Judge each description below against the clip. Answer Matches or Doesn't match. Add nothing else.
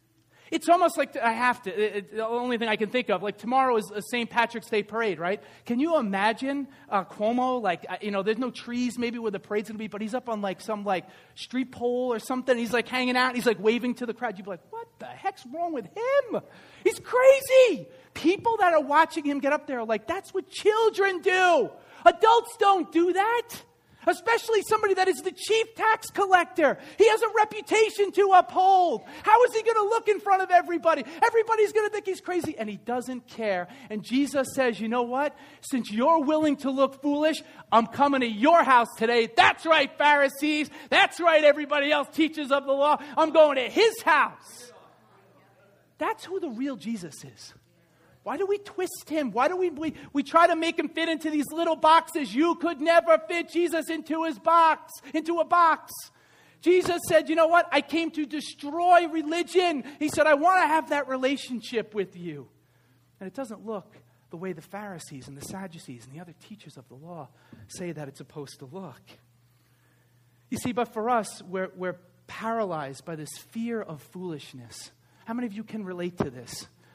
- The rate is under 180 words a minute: Doesn't match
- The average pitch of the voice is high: Matches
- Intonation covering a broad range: Matches